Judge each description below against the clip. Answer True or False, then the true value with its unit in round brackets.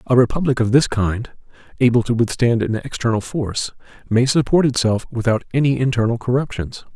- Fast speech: False (155 wpm)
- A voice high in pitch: False (120 Hz)